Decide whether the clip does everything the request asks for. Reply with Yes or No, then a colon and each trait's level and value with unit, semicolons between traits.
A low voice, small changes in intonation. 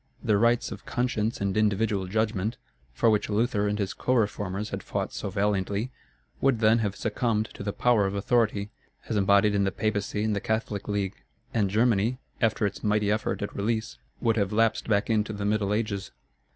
Yes: low, 105 Hz; narrow, 1.8 semitones